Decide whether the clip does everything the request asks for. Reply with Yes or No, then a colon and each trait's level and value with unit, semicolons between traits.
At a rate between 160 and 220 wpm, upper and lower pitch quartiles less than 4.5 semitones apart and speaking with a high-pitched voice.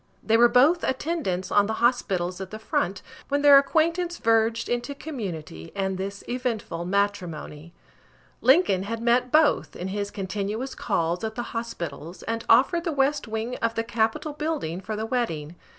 No: average, 165 wpm; average, 5.3 semitones; high, 225 Hz